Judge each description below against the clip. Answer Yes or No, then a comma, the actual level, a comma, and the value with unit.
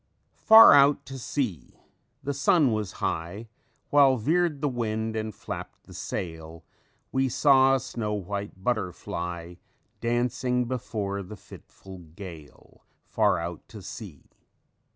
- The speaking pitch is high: No, low, 110 Hz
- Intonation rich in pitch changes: Yes, wide, 6.4 semitones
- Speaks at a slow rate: Yes, slow, 125 wpm